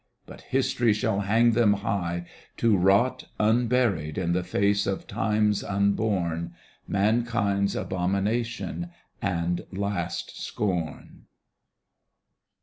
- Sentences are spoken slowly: Yes, slow, 95 wpm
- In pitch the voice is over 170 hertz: No, low, 100 Hz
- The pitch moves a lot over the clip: No, average, 3.2 semitones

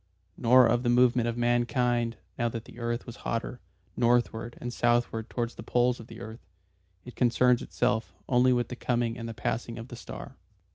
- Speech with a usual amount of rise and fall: No, narrow, 1.0 semitones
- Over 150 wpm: Yes, average, 190 wpm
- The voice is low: Yes, low, 120 Hz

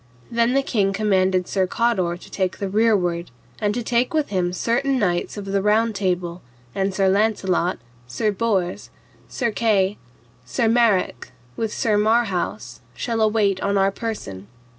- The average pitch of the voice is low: No, high, 200 Hz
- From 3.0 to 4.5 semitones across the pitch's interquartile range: Yes, average, 3.4 semitones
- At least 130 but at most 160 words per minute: Yes, average, 155 wpm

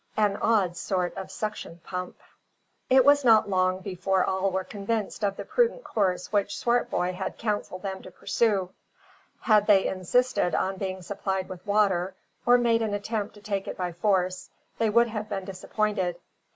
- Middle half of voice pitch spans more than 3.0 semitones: No, narrow, 2.6 semitones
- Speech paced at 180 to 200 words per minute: No, average, 170 wpm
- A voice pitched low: No, high, 200 Hz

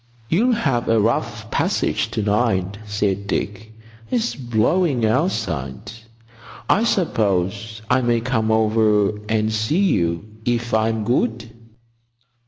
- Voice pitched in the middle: No, low, 110 Hz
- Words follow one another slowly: Yes, slow, 115 wpm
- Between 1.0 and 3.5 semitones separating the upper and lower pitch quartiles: Yes, average, 2.7 semitones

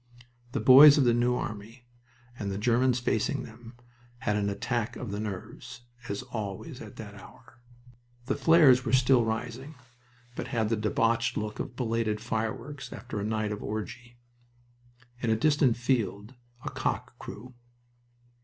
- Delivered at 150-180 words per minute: Yes, average, 155 wpm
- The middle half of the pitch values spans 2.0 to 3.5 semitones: Yes, average, 2.9 semitones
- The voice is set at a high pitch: No, low, 115 Hz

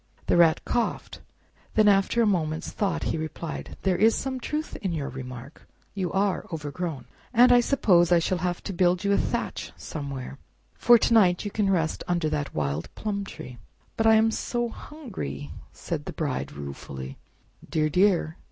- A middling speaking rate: Yes, average, 170 wpm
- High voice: No, medium, 175 Hz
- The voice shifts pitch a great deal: Yes, wide, 5.8 semitones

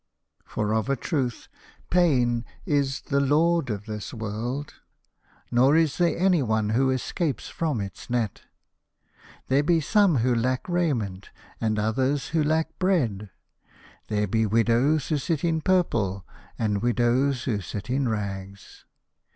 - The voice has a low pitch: Yes, low, 125 Hz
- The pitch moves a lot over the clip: Yes, wide, 5.8 semitones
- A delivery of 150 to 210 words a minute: No, slow, 135 wpm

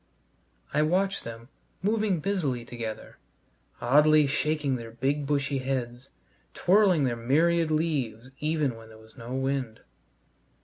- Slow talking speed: Yes, slow, 125 wpm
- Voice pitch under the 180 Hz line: Yes, medium, 140 Hz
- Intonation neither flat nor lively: Yes, average, 4.6 semitones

